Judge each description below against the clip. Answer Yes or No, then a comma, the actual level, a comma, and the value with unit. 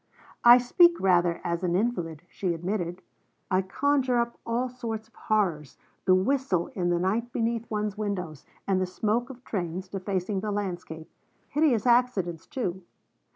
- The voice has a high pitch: Yes, high, 200 Hz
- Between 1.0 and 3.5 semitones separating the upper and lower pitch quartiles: No, average, 4.9 semitones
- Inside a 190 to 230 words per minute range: No, average, 155 wpm